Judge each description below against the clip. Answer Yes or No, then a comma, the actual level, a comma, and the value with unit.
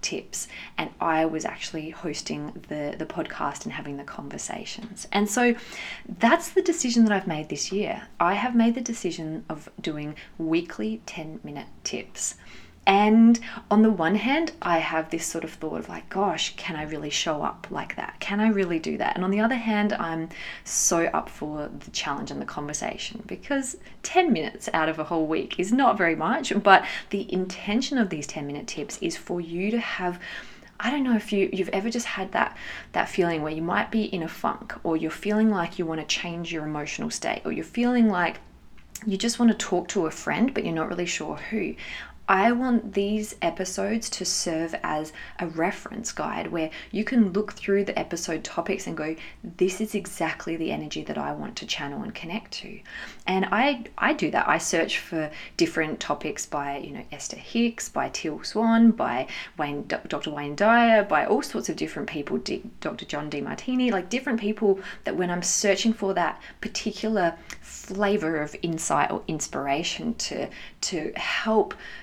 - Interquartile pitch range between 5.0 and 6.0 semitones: Yes, wide, 5.5 semitones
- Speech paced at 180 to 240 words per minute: Yes, average, 190 wpm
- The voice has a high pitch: Yes, high, 195 Hz